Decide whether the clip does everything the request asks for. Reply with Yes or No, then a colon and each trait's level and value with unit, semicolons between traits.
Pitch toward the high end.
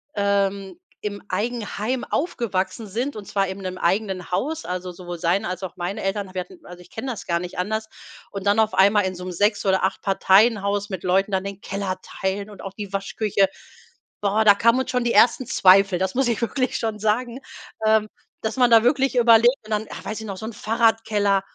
Yes: high, 205 Hz